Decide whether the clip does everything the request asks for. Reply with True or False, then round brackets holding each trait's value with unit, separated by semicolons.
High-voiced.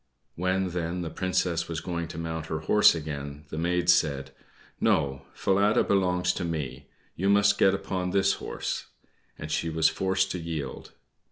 False (85 Hz)